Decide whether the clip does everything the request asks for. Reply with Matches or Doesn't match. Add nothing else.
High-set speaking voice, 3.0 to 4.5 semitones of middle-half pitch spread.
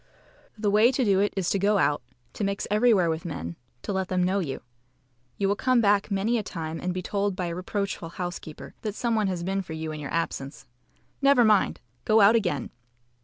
Matches